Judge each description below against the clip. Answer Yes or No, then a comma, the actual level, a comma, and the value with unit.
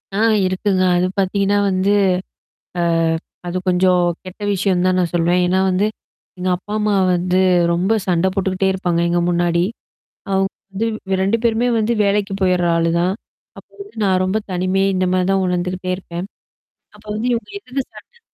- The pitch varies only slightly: Yes, narrow, 1.8 semitones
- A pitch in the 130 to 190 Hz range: Yes, medium, 185 Hz